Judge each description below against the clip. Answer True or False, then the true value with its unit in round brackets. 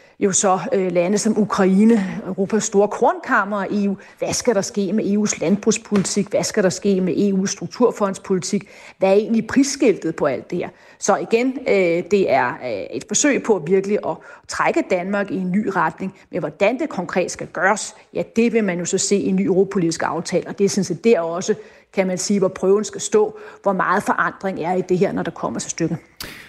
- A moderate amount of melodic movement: False (2.2 semitones)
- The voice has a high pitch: True (200 Hz)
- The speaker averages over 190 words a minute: True (205 wpm)